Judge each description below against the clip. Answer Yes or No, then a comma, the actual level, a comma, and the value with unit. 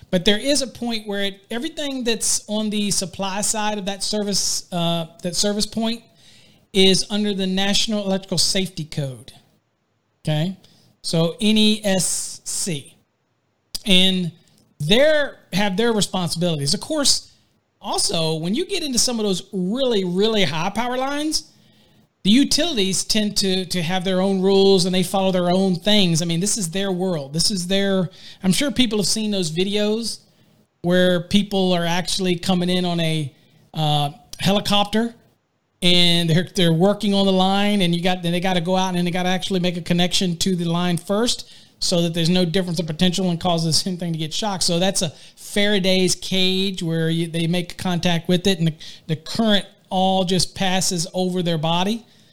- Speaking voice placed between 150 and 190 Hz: Yes, medium, 185 Hz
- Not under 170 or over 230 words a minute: Yes, average, 175 wpm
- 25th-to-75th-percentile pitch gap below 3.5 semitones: Yes, average, 2.8 semitones